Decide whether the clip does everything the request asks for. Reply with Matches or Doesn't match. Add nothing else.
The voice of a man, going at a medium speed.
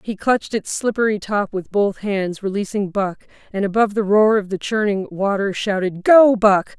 Doesn't match